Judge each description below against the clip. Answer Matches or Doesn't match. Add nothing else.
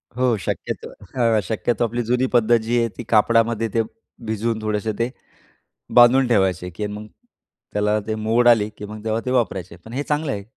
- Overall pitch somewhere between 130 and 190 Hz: Doesn't match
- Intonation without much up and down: Matches